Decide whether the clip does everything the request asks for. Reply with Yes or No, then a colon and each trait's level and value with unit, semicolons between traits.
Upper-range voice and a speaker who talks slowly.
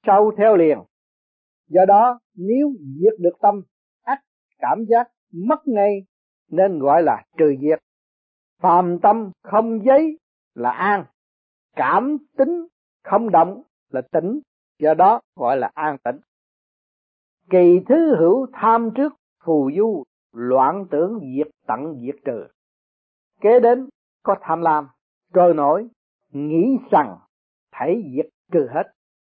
Yes: high, 200 Hz; slow, 130 wpm